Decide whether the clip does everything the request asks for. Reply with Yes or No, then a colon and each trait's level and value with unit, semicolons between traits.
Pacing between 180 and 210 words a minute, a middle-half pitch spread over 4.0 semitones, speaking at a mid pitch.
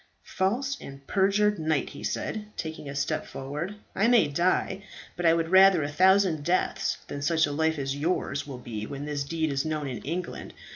Yes: average, 195 wpm; average, 4.8 semitones; medium, 160 Hz